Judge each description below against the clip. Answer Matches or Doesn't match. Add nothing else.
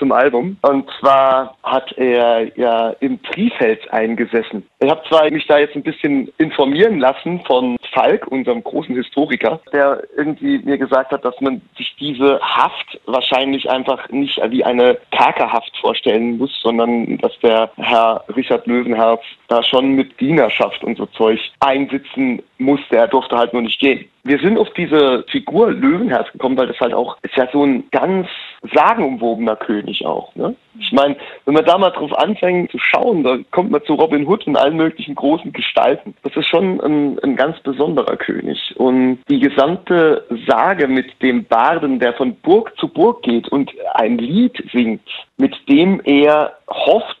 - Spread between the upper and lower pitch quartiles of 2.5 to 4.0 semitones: Doesn't match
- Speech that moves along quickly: Doesn't match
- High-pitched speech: Doesn't match